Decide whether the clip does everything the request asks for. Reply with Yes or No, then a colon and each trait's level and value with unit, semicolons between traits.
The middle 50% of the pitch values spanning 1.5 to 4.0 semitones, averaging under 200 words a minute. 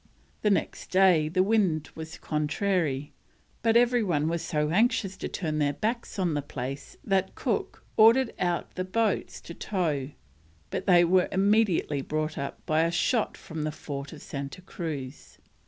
No: average, 4.7 semitones; average, 165 wpm